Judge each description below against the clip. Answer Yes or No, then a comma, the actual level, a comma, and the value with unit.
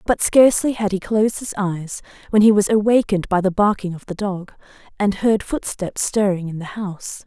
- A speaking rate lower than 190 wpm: No, average, 200 wpm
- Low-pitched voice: No, high, 200 Hz